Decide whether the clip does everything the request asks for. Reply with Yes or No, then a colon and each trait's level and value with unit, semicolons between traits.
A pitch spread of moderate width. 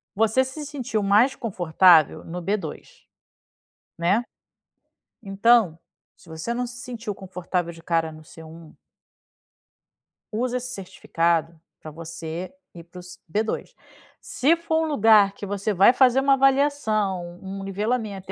No: wide, 5.9 semitones